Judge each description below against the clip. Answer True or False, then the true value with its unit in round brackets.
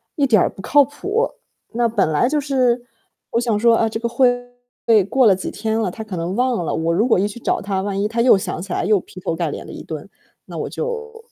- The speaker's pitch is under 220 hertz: False (225 Hz)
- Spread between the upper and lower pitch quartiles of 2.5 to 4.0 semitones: False (4.5 semitones)